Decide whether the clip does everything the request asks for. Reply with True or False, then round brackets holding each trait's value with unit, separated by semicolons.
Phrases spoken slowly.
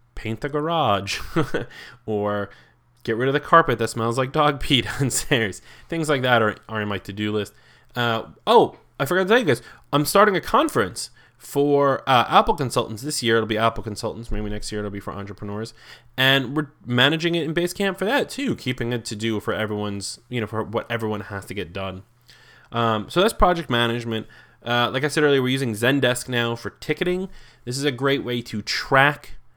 False (205 wpm)